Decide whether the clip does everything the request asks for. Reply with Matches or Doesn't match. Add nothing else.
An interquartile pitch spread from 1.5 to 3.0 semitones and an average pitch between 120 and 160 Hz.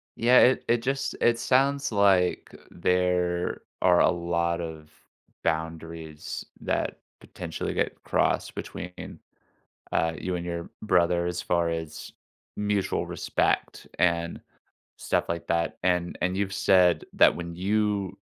Doesn't match